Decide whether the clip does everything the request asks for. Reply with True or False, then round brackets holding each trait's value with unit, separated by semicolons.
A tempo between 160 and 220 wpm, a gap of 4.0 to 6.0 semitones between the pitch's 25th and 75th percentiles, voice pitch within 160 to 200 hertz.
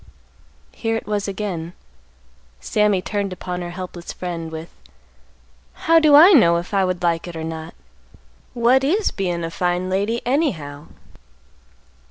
False (145 wpm; 4.8 semitones; 185 Hz)